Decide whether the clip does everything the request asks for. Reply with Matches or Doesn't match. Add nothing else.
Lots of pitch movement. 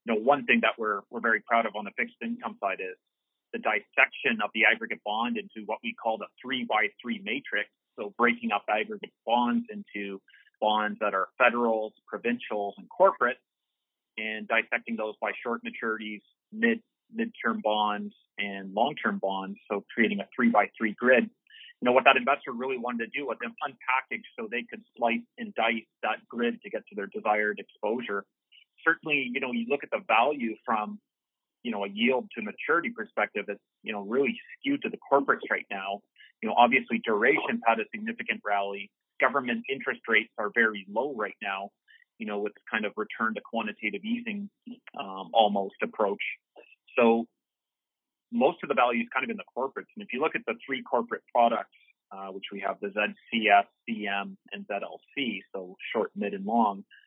Matches